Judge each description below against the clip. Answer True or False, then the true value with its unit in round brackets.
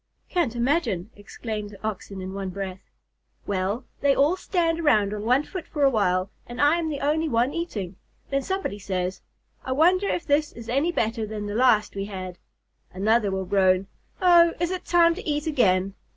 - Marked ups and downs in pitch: True (7.8 semitones)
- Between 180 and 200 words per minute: True (190 wpm)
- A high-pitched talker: True (235 Hz)